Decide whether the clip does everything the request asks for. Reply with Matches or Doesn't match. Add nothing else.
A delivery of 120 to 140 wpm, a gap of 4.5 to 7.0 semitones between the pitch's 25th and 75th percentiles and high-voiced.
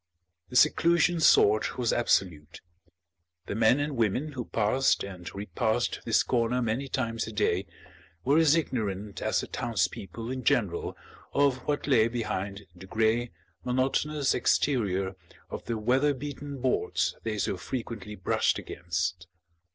Doesn't match